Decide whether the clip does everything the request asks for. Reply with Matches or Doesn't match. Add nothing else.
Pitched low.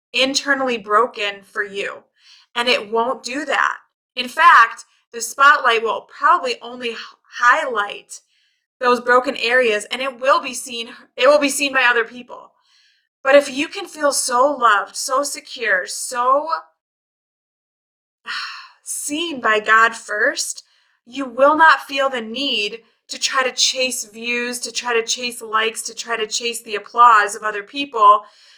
Doesn't match